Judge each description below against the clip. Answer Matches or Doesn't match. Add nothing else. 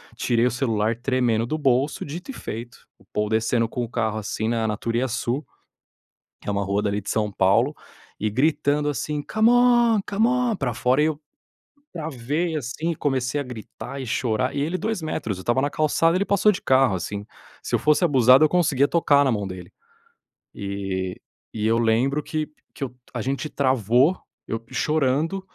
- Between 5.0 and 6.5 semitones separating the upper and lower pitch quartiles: Matches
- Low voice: Matches